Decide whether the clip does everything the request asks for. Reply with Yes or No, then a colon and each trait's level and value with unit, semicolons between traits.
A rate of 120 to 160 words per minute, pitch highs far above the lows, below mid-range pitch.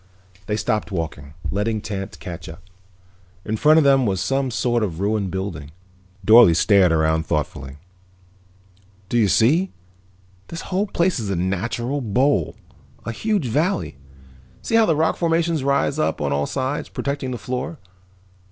Yes: average, 155 wpm; wide, 7.3 semitones; low, 115 Hz